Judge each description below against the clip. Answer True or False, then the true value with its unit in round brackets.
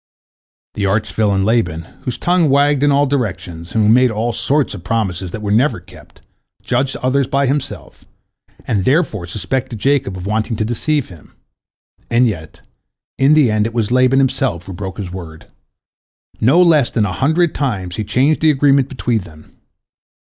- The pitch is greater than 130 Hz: False (115 Hz)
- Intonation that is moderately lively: False (5.9 semitones)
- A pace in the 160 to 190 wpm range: True (175 wpm)